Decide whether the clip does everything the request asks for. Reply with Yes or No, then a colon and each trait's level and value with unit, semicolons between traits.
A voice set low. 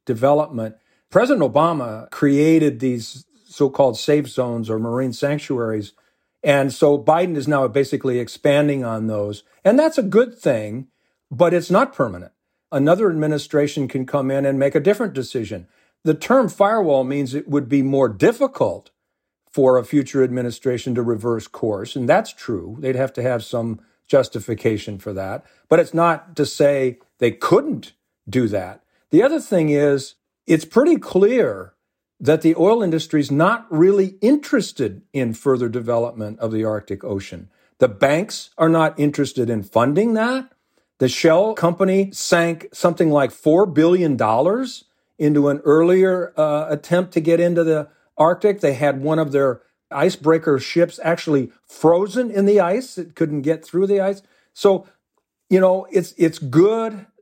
No: medium, 150 Hz